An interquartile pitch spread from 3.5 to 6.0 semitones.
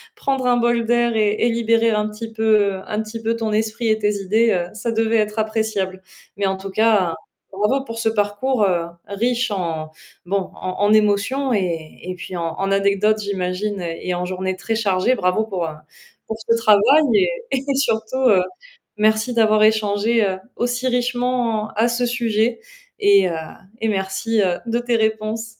No: average, 2.7 semitones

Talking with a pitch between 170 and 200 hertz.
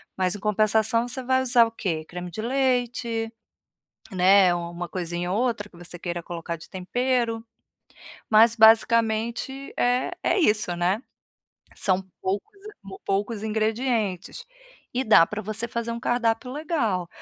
No: high, 220 Hz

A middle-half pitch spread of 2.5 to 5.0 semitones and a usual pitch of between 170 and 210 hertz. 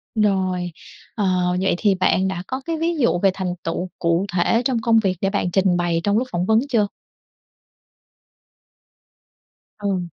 Yes: average, 3.6 semitones; high, 195 Hz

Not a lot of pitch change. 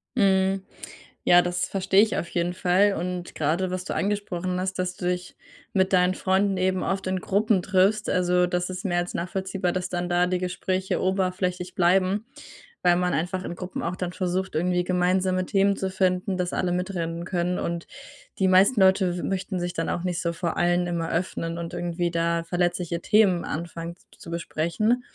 Yes: narrow, 1.2 semitones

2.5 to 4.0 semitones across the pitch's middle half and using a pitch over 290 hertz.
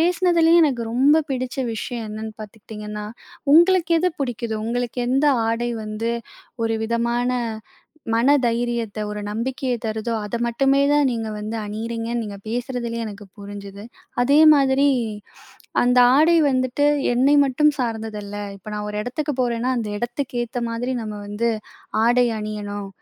No: average, 3.3 semitones; high, 235 Hz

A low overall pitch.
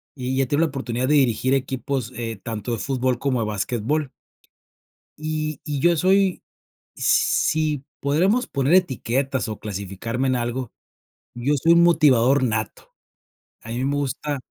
Yes: low, 130 Hz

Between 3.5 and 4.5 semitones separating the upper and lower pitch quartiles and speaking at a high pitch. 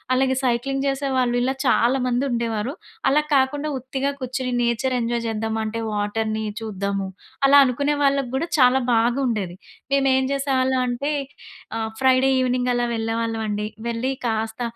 No: average, 2.9 semitones; very high, 250 Hz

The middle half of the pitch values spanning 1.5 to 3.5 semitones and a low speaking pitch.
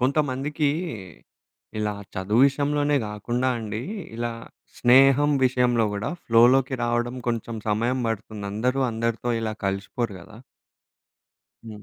Yes: average, 3.2 semitones; low, 120 Hz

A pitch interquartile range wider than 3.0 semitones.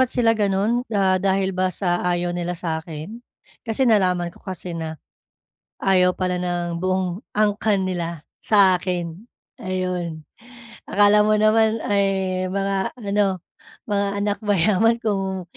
No: narrow, 2.6 semitones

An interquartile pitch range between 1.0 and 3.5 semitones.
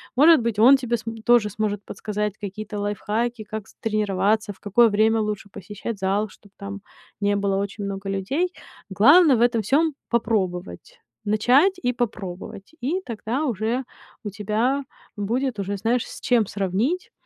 Yes: average, 3.1 semitones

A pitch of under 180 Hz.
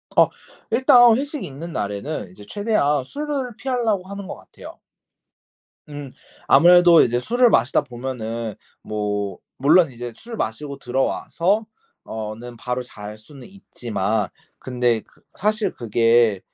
Yes: low, 135 Hz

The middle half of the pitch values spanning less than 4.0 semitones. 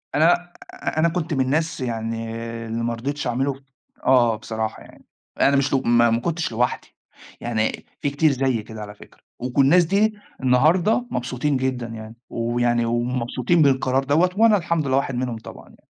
No: average, 4.3 semitones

